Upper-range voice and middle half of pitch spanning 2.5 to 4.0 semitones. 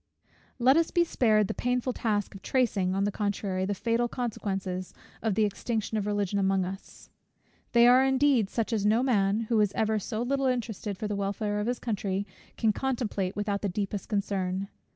Yes: high, 210 Hz; average, 3.3 semitones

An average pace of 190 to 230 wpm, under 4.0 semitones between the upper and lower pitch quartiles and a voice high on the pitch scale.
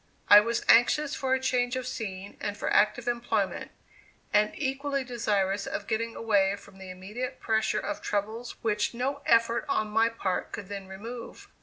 No: average, 170 wpm; average, 3.1 semitones; high, 225 Hz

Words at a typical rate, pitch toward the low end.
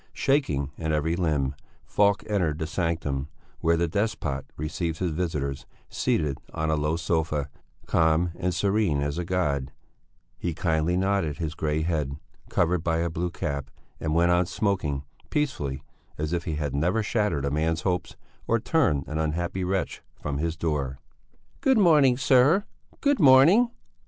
Yes: average, 155 wpm; very low, 85 Hz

